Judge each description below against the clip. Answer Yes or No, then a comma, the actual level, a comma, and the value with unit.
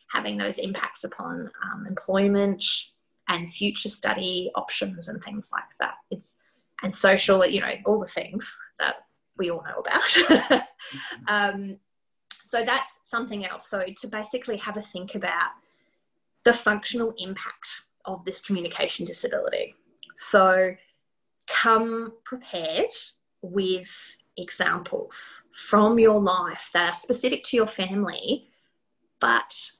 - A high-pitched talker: Yes, high, 205 Hz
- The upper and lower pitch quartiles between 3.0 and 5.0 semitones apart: Yes, average, 3.4 semitones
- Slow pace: Yes, slow, 125 wpm